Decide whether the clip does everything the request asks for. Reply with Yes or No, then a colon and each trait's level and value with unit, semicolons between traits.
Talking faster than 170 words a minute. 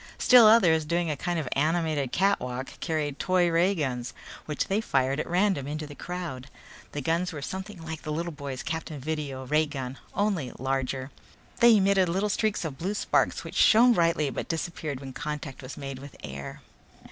Yes: average, 180 wpm